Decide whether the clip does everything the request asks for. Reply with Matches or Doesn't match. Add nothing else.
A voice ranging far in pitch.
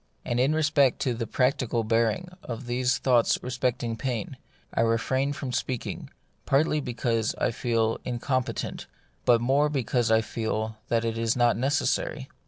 Doesn't match